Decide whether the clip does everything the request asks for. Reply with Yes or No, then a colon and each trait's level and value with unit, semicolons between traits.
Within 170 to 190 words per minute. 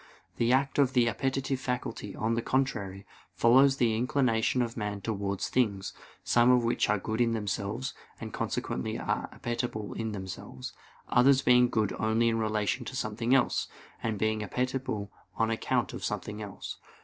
No: average, 160 wpm